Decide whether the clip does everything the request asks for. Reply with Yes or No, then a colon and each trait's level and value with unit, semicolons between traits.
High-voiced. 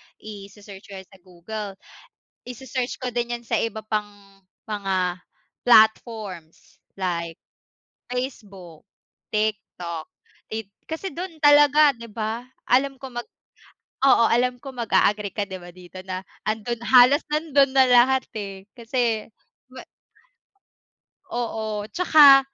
Yes: high, 220 Hz